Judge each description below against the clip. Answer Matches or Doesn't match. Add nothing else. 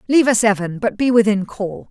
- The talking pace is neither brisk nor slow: Doesn't match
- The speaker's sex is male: Doesn't match